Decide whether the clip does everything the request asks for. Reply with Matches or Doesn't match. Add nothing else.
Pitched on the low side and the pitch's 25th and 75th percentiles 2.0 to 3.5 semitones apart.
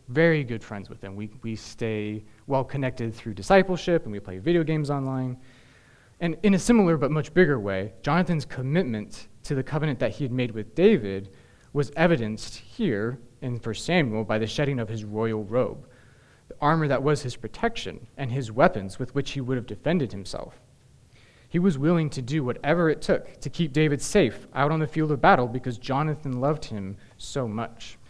Doesn't match